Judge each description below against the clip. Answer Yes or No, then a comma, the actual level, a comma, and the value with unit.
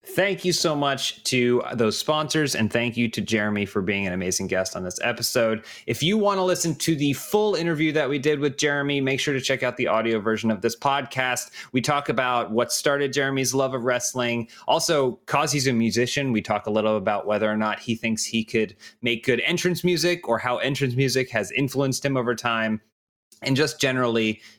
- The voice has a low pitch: Yes, low, 125 Hz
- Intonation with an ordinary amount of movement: Yes, average, 4.1 semitones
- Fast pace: Yes, fast, 210 wpm